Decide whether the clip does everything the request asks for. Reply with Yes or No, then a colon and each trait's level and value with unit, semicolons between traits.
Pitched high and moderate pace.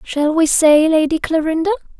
Yes: very high, 320 Hz; average, 150 wpm